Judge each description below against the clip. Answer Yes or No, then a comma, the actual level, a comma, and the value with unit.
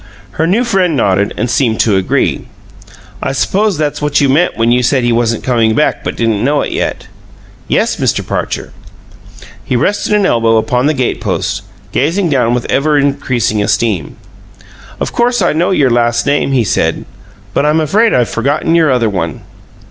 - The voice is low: Yes, low, 130 Hz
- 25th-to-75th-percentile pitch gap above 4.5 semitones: Yes, average, 5.1 semitones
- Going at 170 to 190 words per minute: Yes, average, 180 wpm